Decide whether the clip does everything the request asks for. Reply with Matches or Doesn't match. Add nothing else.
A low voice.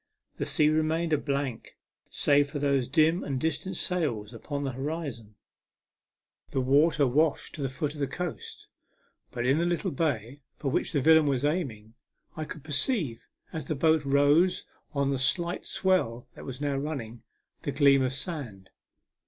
Doesn't match